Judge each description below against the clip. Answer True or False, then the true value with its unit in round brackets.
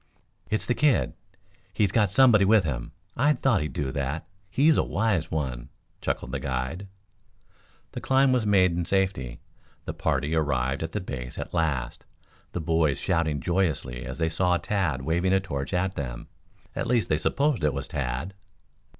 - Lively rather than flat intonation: True (6.3 semitones)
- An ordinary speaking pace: True (175 wpm)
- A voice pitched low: True (85 Hz)